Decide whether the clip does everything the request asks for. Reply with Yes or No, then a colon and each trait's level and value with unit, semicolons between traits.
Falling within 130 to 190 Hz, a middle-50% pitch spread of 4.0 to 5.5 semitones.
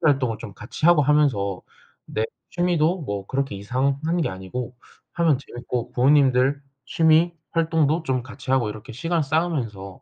Yes: low, 135 Hz; average, 5.2 semitones